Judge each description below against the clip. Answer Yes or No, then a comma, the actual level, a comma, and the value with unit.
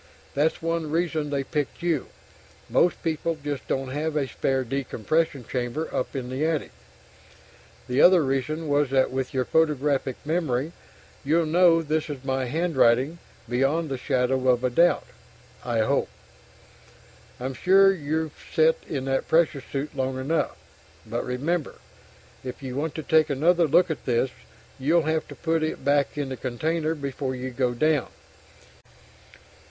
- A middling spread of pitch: Yes, average, 3.5 semitones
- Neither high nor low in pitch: Yes, medium, 145 Hz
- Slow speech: No, average, 155 wpm